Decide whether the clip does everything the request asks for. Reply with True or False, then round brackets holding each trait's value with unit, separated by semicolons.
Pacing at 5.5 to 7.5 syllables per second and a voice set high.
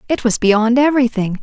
True (5.6 syllables/s; 240 Hz)